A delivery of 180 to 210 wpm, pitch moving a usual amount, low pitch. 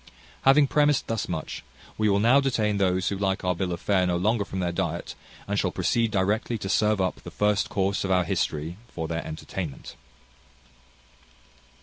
Yes: average, 185 wpm; average, 3.1 semitones; very low, 95 Hz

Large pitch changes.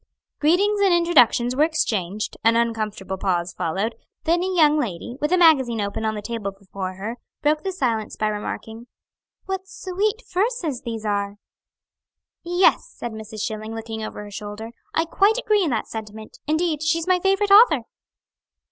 Yes: wide, 8.5 semitones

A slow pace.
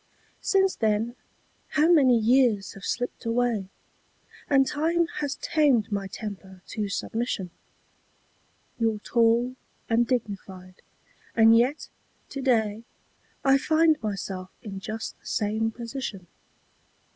Yes: slow, 110 wpm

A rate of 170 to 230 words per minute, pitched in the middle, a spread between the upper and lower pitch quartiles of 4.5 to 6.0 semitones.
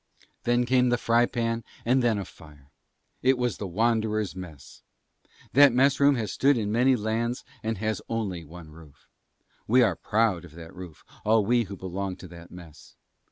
No: average, 180 wpm; low, 110 Hz; average, 5.2 semitones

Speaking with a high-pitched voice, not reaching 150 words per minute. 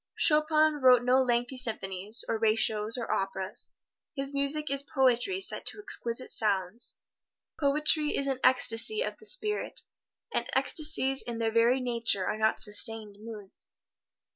Yes: high, 245 Hz; average, 140 wpm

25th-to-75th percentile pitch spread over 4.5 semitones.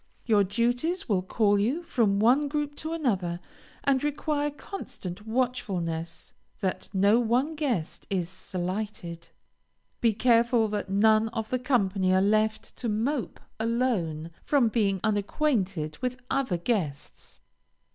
Yes: average, 5.0 semitones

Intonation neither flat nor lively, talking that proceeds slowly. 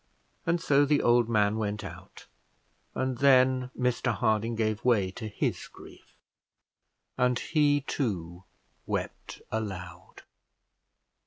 Yes: average, 3.9 semitones; slow, 110 wpm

